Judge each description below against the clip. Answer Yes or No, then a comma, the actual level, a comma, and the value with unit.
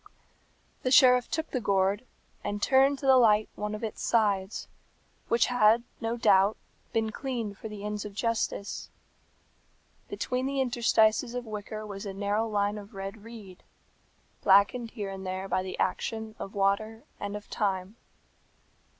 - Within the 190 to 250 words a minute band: No, average, 155 wpm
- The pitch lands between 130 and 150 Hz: No, high, 215 Hz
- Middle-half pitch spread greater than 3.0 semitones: No, narrow, 2.6 semitones